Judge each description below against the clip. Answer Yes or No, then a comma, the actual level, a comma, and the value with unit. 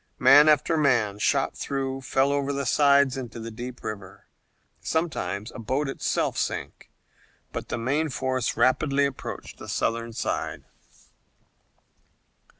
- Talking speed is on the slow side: Yes, slow, 130 wpm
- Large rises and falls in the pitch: No, average, 3.4 semitones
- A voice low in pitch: Yes, low, 130 Hz